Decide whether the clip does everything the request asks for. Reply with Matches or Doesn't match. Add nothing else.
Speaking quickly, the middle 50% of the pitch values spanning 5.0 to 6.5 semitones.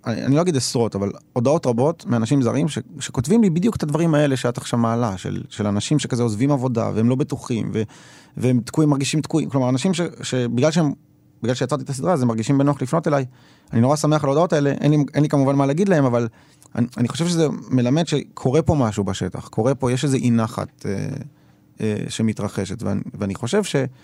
Doesn't match